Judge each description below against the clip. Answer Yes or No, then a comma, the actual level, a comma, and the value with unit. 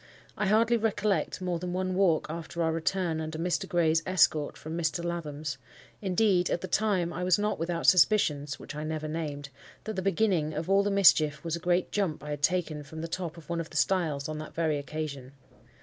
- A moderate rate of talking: No, fast, 210 wpm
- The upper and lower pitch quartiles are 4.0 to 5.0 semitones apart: No, average, 3.1 semitones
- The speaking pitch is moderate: Yes, medium, 170 Hz